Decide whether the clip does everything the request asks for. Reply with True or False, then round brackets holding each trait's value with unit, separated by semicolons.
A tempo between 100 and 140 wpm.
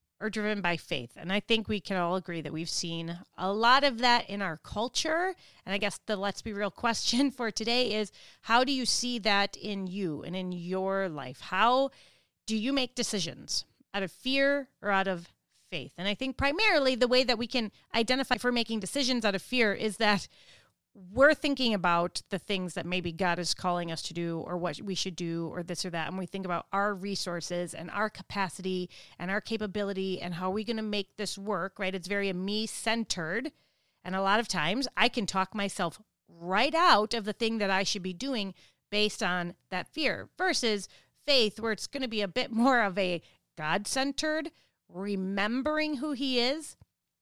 False (205 wpm)